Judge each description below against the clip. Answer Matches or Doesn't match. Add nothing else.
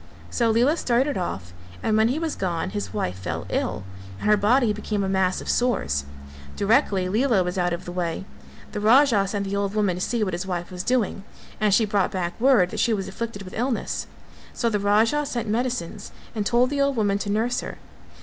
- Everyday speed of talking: Doesn't match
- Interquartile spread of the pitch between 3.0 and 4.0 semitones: Doesn't match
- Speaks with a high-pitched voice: Matches